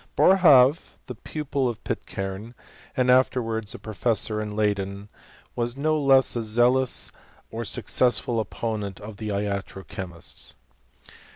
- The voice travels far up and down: No, average, 3.7 semitones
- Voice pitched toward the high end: No, low, 115 Hz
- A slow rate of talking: Yes, slow, 125 wpm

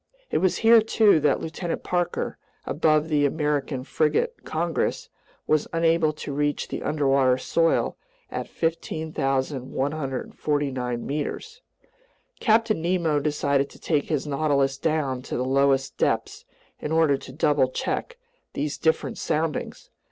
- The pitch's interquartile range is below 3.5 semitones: Yes, average, 2.9 semitones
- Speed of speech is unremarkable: No, slow, 125 wpm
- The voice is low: No, medium, 150 Hz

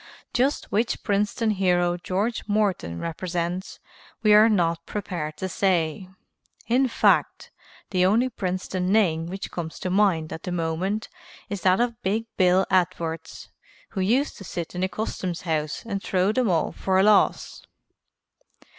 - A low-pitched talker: No, medium, 185 Hz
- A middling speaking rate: Yes, average, 150 wpm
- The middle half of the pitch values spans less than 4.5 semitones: Yes, average, 3.3 semitones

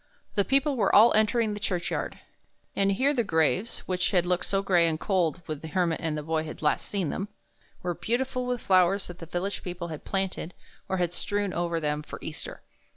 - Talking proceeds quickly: Yes, fast, 215 wpm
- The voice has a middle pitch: Yes, medium, 180 Hz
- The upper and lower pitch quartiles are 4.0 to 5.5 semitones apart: No, average, 3.5 semitones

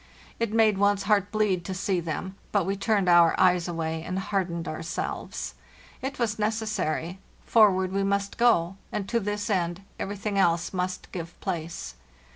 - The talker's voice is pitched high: Yes, high, 195 Hz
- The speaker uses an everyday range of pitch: Yes, average, 3.1 semitones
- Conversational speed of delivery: Yes, average, 165 wpm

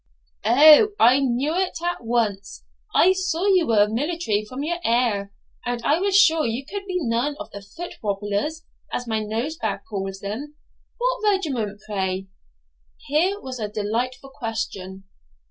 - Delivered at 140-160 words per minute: Yes, average, 150 wpm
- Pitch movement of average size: No, wide, 7.5 semitones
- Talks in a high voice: Yes, high, 245 Hz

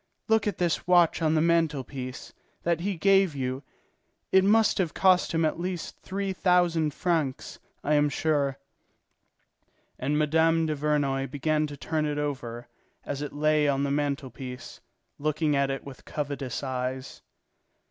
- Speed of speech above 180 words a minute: No, average, 155 wpm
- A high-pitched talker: No, medium, 150 Hz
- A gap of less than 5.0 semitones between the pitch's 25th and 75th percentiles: Yes, average, 3.3 semitones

